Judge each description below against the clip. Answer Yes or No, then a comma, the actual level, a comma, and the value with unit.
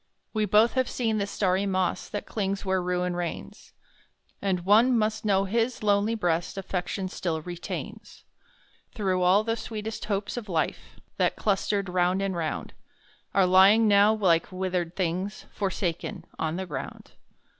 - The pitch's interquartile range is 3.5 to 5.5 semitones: No, average, 2.8 semitones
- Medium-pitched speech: No, high, 195 Hz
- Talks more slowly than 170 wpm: Yes, average, 150 wpm